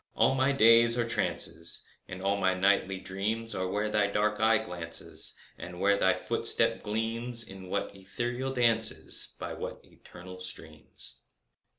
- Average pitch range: Yes, average, 3.6 semitones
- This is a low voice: Yes, low, 100 Hz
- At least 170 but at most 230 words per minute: No, average, 155 wpm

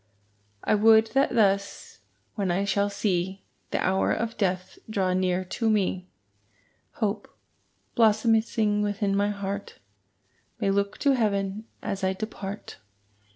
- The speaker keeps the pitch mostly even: Yes, narrow, 2.0 semitones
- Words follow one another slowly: Yes, slow, 125 wpm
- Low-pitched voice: No, high, 200 Hz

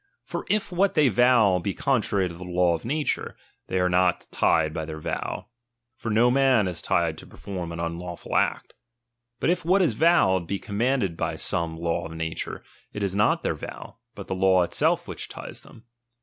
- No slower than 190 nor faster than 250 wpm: Yes, average, 200 wpm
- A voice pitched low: Yes, very low, 95 Hz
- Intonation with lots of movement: Yes, wide, 6.5 semitones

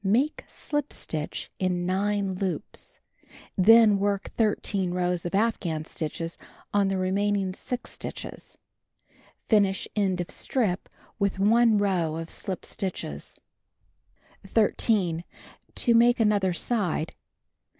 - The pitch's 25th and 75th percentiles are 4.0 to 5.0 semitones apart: No, average, 2.9 semitones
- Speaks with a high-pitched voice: Yes, high, 195 Hz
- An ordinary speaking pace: No, slow, 115 wpm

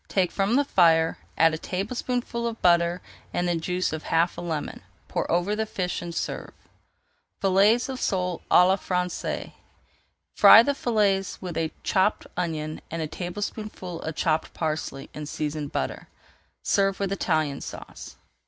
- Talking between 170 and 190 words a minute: No, average, 155 wpm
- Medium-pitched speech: Yes, medium, 180 Hz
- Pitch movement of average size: Yes, average, 3.4 semitones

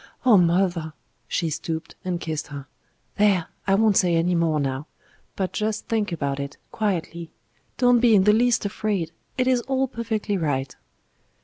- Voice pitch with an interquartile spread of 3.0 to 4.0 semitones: No, average, 5.2 semitones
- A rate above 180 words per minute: No, average, 165 wpm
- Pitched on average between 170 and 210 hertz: Yes, medium, 185 Hz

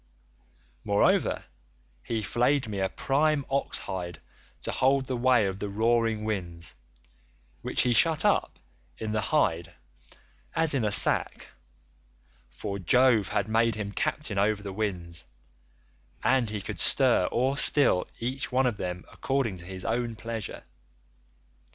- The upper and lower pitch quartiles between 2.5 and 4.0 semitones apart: No, average, 5.0 semitones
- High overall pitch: No, low, 110 Hz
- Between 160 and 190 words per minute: No, average, 140 wpm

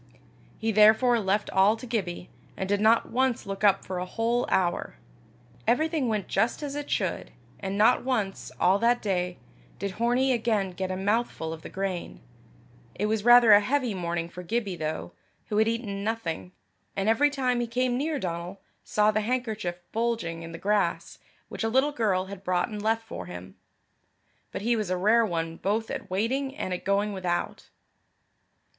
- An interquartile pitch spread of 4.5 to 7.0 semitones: No, average, 4.0 semitones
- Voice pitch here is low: No, high, 210 Hz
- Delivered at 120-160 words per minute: No, average, 180 wpm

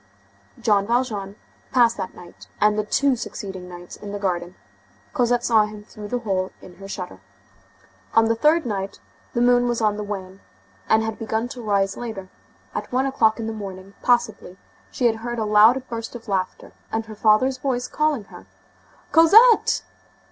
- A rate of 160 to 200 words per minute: Yes, average, 175 wpm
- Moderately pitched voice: No, high, 220 Hz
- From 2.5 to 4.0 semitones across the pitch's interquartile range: Yes, average, 3.5 semitones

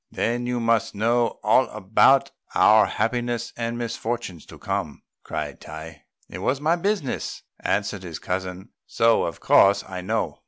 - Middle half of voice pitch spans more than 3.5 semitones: Yes, average, 4.1 semitones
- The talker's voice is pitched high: No, low, 115 Hz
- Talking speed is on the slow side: No, average, 150 wpm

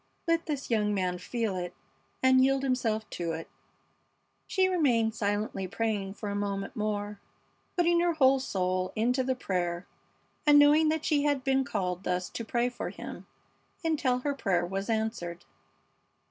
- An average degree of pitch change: No, wide, 5.8 semitones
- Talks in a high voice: Yes, high, 225 Hz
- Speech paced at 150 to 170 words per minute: Yes, average, 160 wpm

